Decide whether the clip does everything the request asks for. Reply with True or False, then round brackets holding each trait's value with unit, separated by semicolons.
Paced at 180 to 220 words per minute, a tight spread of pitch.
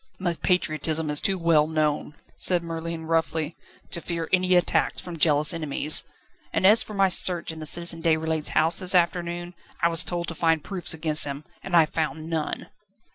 True (185 wpm; 1.9 semitones)